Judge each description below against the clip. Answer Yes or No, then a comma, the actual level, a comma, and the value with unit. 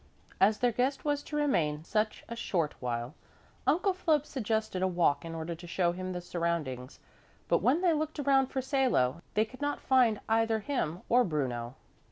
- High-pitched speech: Yes, high, 215 Hz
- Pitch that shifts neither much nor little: No, wide, 8.3 semitones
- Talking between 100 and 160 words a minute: No, average, 185 wpm